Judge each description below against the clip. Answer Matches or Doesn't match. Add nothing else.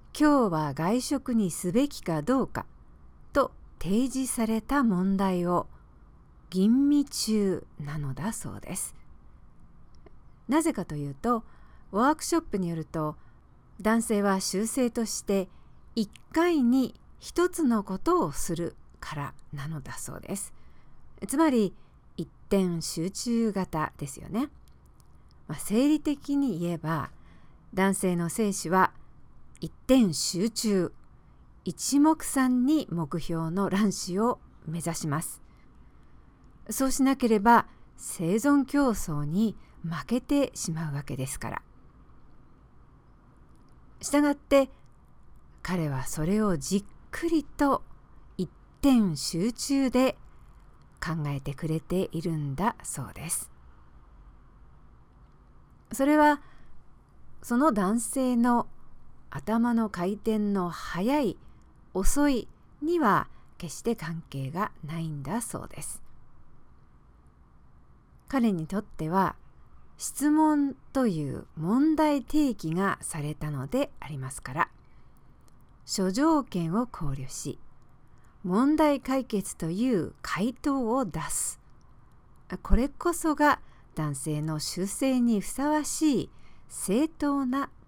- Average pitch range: Doesn't match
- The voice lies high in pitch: Matches